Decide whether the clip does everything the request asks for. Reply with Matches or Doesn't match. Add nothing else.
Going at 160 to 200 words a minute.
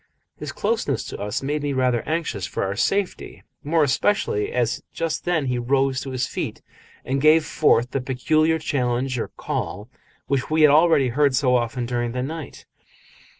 Matches